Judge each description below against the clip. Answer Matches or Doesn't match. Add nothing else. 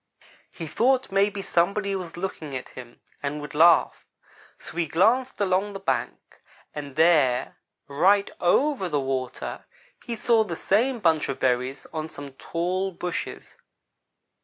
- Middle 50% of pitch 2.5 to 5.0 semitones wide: Doesn't match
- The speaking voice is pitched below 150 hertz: Doesn't match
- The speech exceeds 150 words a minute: Doesn't match